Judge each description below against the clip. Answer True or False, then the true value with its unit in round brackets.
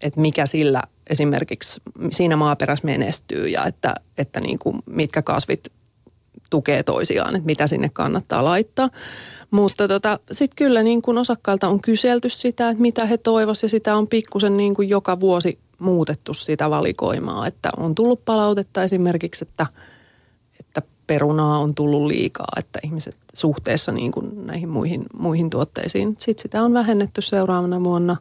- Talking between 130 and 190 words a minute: True (150 wpm)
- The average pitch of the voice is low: False (190 Hz)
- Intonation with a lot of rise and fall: True (6.2 semitones)